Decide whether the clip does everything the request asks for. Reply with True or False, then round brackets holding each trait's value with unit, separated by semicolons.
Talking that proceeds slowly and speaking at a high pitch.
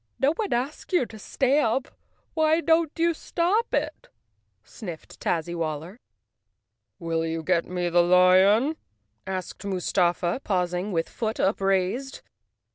True (120 wpm; 195 Hz)